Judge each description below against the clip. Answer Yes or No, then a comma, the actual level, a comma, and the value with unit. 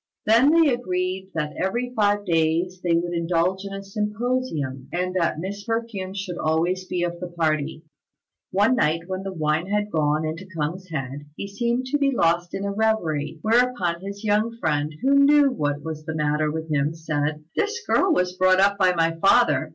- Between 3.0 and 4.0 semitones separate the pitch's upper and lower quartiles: No, average, 4.6 semitones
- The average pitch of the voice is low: No, medium, 185 Hz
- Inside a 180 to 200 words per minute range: Yes, average, 190 wpm